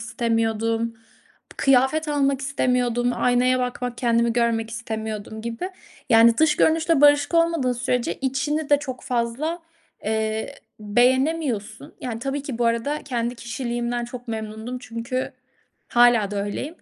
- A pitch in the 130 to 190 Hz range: No, high, 245 Hz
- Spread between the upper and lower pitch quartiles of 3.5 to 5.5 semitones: No, average, 2.9 semitones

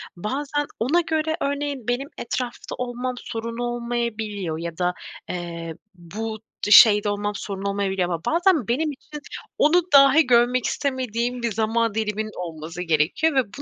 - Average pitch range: Yes, average, 5.0 semitones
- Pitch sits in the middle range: No, high, 230 Hz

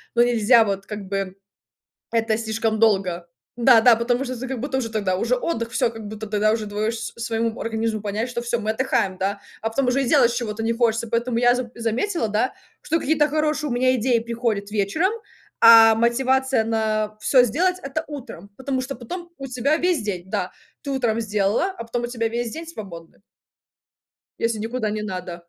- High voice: Yes, high, 230 Hz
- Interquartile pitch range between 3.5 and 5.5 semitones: No, average, 2.9 semitones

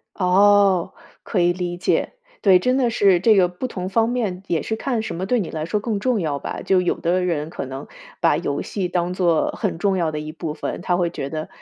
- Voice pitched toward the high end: No, medium, 180 Hz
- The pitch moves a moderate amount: Yes, average, 3.2 semitones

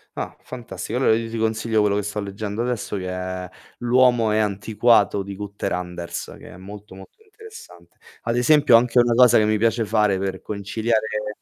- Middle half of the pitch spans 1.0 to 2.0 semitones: No, average, 2.8 semitones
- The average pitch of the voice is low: Yes, low, 105 Hz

